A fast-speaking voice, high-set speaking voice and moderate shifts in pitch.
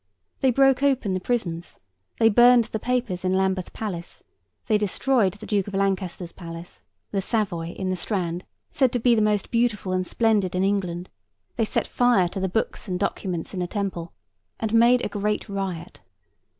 No: average, 180 wpm; high, 200 Hz; average, 3.7 semitones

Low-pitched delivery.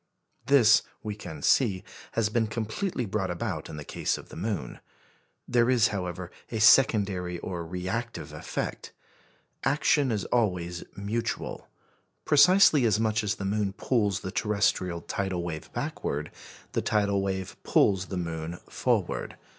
Yes: low, 100 Hz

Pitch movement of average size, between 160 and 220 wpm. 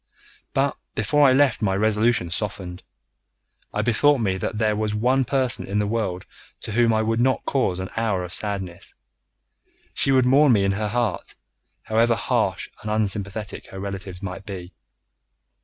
Yes: average, 3.5 semitones; average, 165 wpm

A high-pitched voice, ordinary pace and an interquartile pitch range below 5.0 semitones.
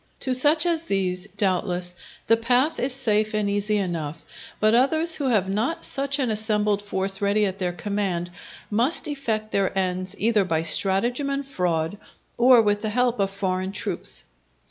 Yes: high, 210 Hz; average, 165 wpm; average, 4.6 semitones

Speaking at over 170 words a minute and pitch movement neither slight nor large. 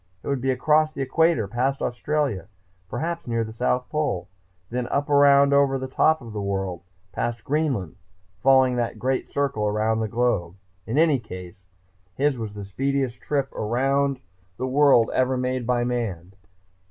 No: average, 165 wpm; average, 4.0 semitones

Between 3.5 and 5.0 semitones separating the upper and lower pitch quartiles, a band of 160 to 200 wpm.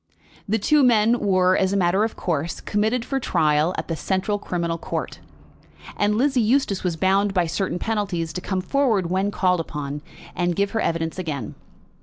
Yes: average, 3.8 semitones; average, 180 wpm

